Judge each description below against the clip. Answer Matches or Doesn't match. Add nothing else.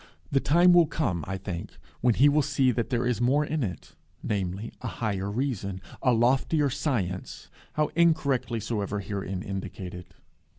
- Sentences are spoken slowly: Doesn't match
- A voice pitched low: Matches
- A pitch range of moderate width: Doesn't match